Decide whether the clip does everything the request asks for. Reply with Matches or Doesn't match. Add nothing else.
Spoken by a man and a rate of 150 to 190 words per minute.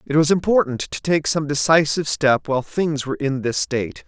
Doesn't match